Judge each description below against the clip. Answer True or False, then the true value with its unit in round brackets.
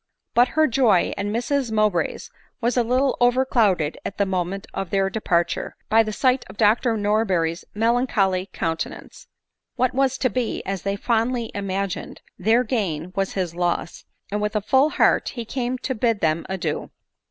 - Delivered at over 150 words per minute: True (170 wpm)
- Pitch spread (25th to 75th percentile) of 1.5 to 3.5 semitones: False (4.3 semitones)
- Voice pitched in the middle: False (215 Hz)